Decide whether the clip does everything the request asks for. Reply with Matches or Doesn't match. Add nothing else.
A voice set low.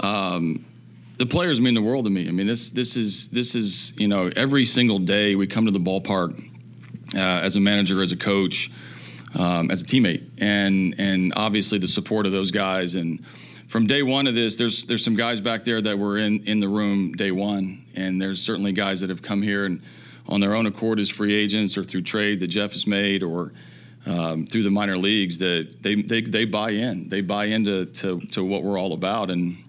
Matches